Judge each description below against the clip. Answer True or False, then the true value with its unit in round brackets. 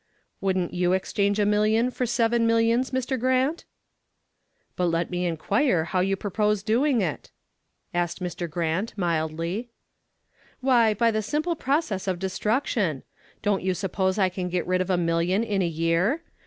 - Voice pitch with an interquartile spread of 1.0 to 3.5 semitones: False (4.6 semitones)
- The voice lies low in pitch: False (195 Hz)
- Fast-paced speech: False (155 wpm)